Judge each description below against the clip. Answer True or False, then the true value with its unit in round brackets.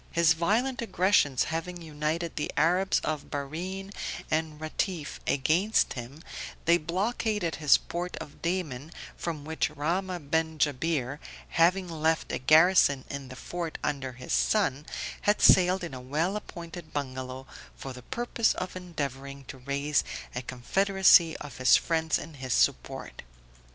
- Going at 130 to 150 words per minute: True (140 wpm)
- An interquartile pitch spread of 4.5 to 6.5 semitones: False (4.1 semitones)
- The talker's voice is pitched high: False (160 Hz)